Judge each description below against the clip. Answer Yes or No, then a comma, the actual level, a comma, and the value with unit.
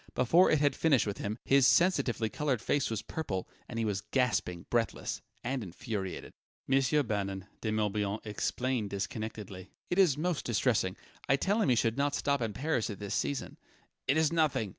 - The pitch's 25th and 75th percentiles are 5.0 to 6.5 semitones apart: Yes, average, 5.3 semitones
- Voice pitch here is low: Yes, low, 120 Hz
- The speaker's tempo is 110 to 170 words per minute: No, average, 185 wpm